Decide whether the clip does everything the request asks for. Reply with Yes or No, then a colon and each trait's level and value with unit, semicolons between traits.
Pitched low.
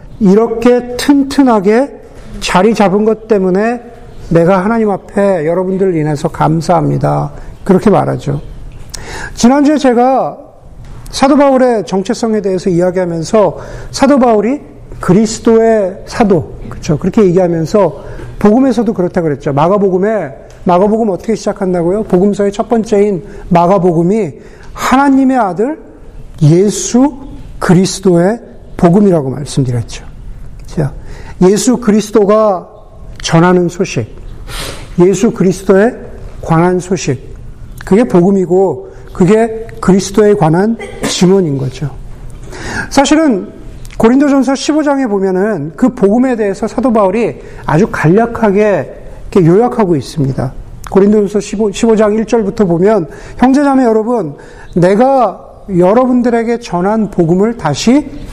No: high, 200 Hz